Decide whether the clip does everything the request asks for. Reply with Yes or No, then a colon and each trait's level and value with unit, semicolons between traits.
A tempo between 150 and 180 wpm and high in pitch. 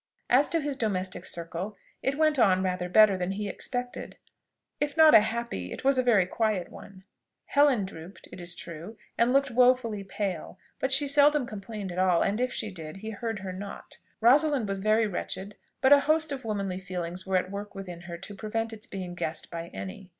No: average, 200 wpm; high, 205 Hz